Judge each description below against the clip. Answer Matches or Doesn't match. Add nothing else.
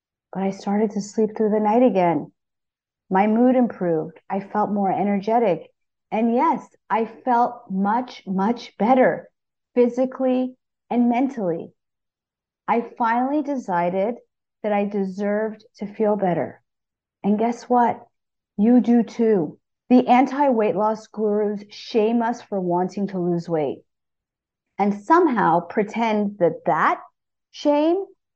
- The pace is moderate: Doesn't match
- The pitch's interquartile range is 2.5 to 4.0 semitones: Matches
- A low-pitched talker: Doesn't match